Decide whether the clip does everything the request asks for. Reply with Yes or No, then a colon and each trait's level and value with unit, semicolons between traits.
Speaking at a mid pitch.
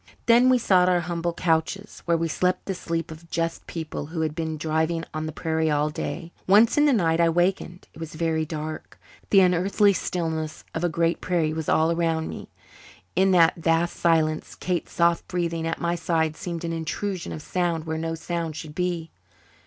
Yes: medium, 165 Hz